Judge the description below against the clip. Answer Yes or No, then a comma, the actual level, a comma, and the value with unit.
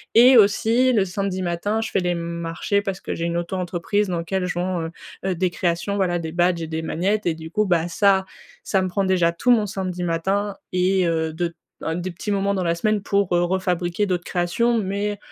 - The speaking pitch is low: No, medium, 185 Hz